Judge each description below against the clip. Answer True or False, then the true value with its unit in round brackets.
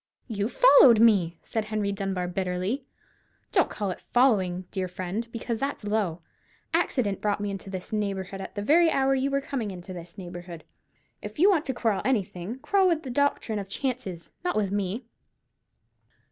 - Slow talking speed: False (175 wpm)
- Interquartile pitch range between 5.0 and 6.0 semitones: True (5.5 semitones)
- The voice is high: True (205 Hz)